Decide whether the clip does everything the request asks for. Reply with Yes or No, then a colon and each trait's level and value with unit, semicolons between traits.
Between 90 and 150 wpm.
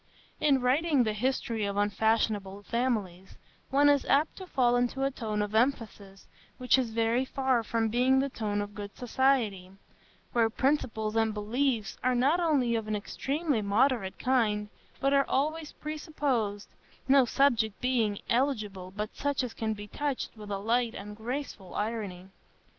No: average, 160 wpm